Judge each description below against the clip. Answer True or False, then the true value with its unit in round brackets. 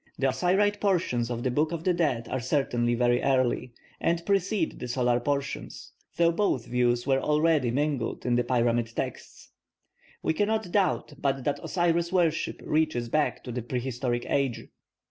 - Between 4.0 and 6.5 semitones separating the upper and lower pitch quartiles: True (5.5 semitones)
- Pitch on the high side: False (135 Hz)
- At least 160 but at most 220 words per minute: True (165 wpm)